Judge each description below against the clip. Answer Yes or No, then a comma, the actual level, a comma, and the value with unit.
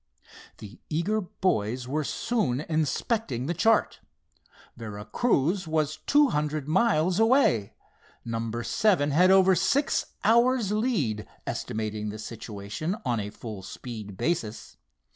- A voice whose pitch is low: No, medium, 155 Hz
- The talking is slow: Yes, slow, 120 wpm